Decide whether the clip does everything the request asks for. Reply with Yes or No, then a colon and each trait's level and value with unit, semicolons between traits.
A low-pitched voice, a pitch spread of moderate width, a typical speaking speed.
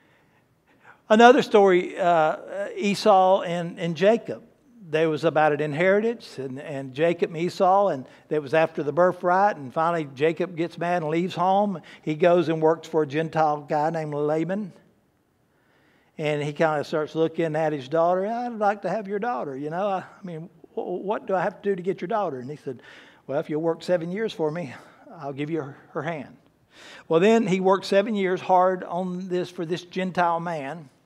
No: medium, 170 Hz; average, 3.6 semitones; average, 190 wpm